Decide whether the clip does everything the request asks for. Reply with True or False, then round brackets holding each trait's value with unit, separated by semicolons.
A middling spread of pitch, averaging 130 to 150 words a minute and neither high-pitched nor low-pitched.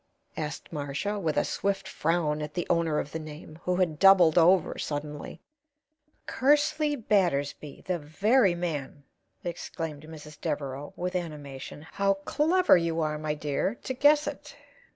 True (4.6 semitones; 145 wpm; 165 Hz)